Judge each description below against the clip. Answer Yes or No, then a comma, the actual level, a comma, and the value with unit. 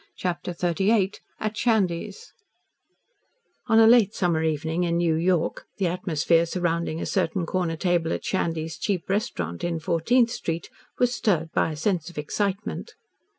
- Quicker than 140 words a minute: Yes, average, 150 wpm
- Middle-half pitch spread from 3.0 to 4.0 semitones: Yes, average, 3.5 semitones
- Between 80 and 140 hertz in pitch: No, medium, 175 Hz